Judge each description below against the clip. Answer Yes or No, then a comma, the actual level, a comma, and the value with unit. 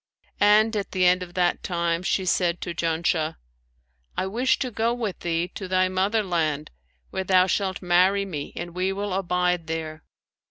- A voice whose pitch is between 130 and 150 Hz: No, medium, 180 Hz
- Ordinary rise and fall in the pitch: No, narrow, 2.2 semitones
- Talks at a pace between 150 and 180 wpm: Yes, average, 175 wpm